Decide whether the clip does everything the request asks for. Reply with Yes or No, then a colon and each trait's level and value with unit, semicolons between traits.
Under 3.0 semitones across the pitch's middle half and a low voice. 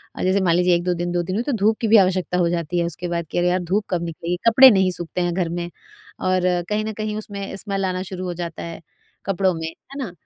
No: narrow, 2.5 semitones; medium, 180 Hz